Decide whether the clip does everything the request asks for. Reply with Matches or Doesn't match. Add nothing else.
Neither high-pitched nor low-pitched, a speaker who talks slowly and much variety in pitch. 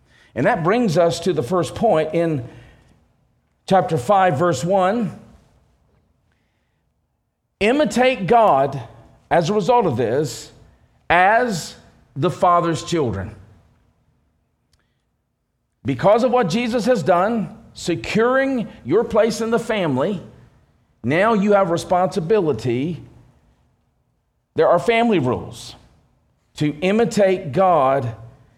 Matches